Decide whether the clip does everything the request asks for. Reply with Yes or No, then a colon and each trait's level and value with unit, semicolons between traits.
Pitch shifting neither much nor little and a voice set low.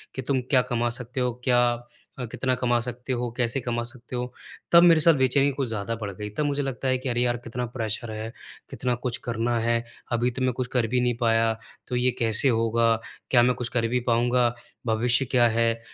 No: narrow, 1.6 semitones; low, 120 Hz